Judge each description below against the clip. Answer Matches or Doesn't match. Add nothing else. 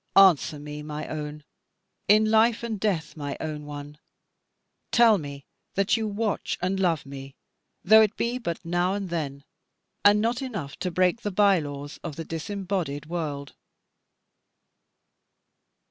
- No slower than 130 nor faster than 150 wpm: Matches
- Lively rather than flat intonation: Matches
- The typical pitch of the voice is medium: Matches